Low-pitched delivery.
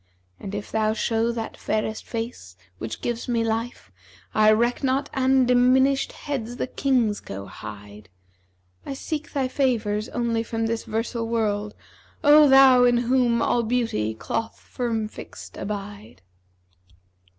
No: high, 230 Hz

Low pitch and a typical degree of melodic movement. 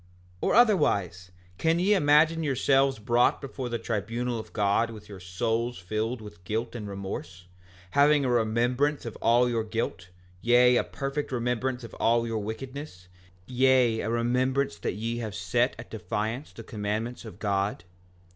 Yes: low, 115 Hz; average, 3.5 semitones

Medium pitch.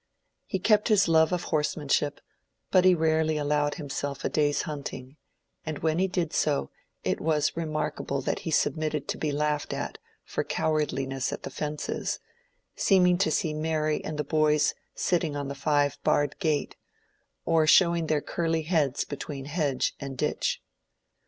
Yes: medium, 155 Hz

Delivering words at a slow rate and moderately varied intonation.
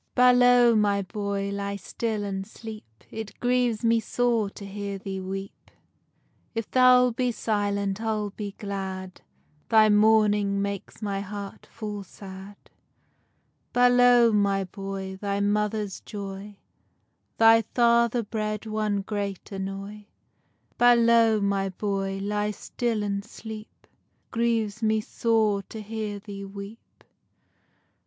No: slow, 120 wpm; narrow, 2.1 semitones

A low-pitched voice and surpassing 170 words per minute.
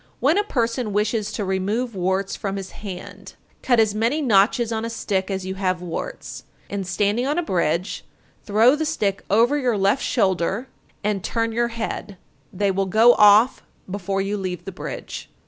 No: high, 205 Hz; average, 180 wpm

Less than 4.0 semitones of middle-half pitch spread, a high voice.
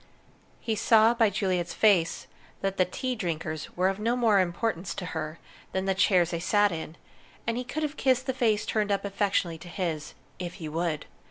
No: average, 4.4 semitones; high, 195 Hz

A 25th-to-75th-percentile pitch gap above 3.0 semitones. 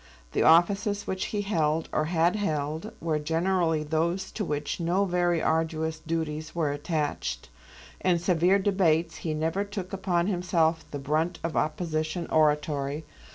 No: average, 2.7 semitones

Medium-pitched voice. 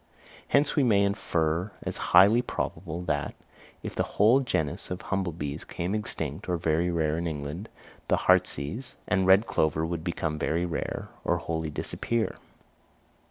No: very low, 85 Hz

